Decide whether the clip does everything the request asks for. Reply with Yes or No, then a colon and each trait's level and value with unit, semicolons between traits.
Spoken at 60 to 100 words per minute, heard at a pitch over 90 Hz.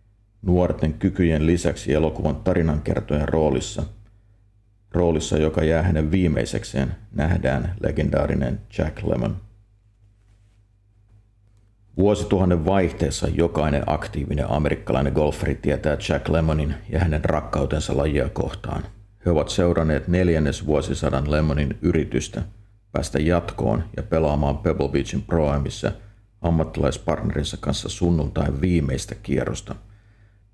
No: slow, 95 wpm; very low, 85 Hz